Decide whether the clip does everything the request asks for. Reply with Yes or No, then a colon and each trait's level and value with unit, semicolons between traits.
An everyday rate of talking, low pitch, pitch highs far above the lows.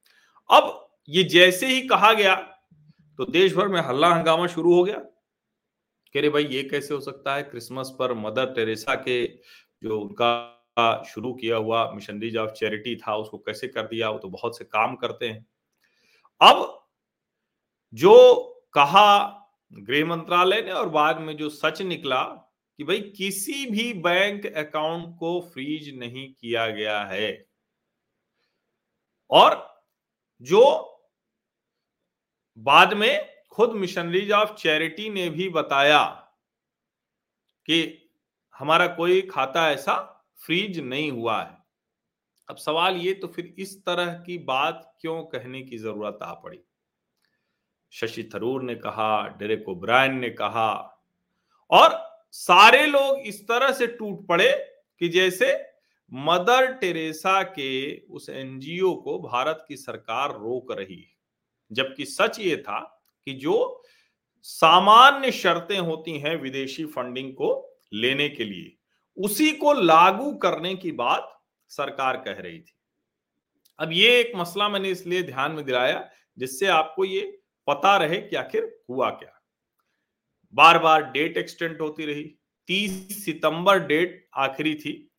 No: average, 135 wpm; medium, 165 Hz; wide, 6.8 semitones